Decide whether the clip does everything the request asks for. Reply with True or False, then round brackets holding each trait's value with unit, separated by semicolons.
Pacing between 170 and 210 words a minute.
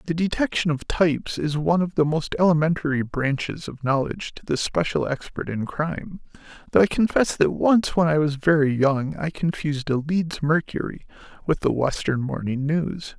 True (180 wpm)